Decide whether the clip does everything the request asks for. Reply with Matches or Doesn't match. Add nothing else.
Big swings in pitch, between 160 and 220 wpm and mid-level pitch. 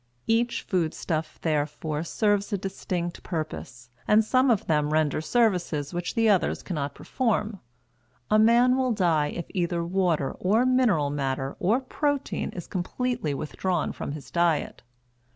Doesn't match